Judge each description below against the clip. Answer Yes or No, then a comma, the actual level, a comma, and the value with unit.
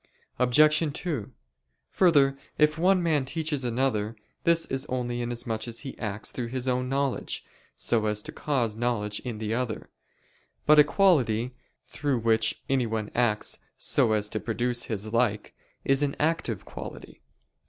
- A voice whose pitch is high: No, low, 125 Hz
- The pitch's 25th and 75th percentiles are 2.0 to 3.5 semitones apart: No, average, 4.2 semitones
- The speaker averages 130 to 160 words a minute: Yes, average, 150 wpm